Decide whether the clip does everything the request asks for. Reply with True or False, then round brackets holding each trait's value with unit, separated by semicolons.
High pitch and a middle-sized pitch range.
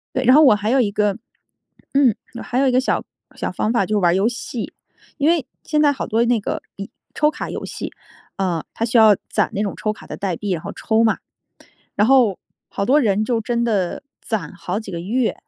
True (220 Hz; 4.0 semitones)